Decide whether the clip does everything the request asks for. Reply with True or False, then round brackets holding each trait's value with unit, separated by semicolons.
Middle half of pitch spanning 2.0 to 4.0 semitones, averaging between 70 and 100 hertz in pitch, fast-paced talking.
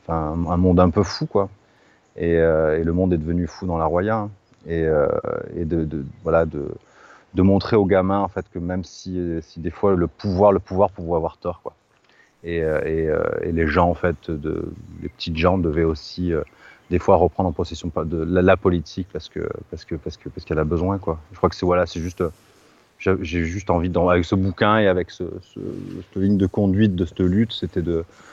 True (2.5 semitones; 90 Hz; 230 wpm)